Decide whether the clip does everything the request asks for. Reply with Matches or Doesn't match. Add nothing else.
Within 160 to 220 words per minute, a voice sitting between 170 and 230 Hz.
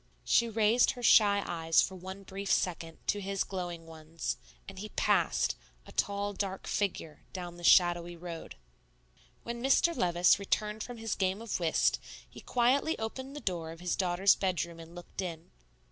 Matches